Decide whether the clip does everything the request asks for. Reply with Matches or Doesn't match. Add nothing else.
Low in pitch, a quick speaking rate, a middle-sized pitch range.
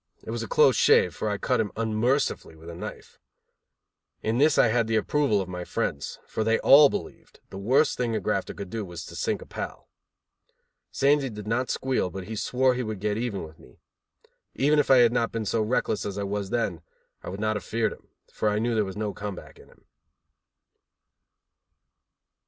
Matches